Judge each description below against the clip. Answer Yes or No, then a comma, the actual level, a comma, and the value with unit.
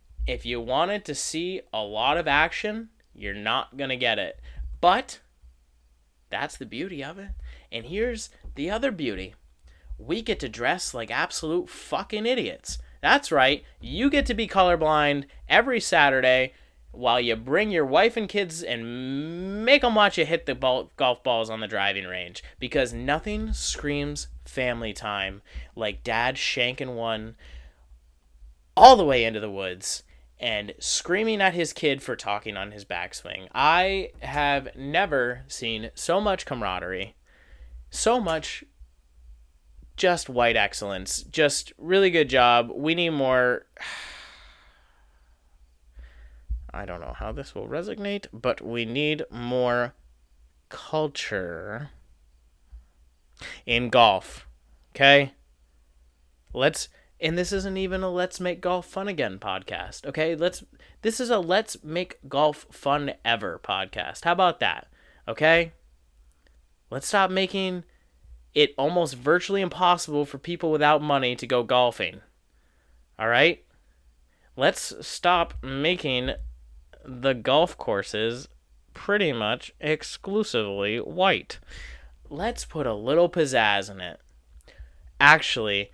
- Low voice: Yes, low, 120 Hz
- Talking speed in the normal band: No, slow, 125 wpm